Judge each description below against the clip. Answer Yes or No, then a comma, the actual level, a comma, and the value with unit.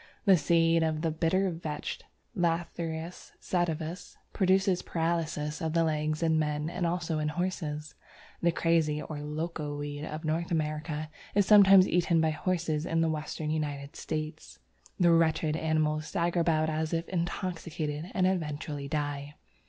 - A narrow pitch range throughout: Yes, narrow, 2.0 semitones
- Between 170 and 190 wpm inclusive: No, average, 145 wpm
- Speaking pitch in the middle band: Yes, medium, 160 Hz